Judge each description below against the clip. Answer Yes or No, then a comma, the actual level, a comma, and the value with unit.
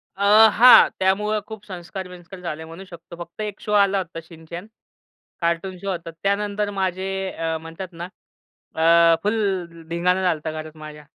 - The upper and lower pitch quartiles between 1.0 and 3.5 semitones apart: Yes, average, 2.9 semitones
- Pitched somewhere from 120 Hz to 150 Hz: No, medium, 180 Hz